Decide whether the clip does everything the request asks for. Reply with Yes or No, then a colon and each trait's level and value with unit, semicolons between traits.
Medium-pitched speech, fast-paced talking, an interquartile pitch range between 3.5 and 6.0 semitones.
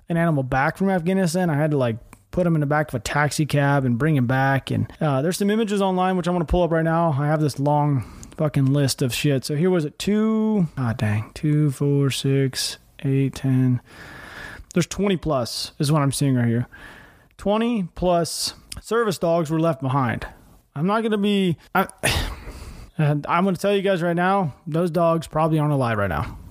Yes: medium, 155 Hz; fast, 210 wpm; average, 4.8 semitones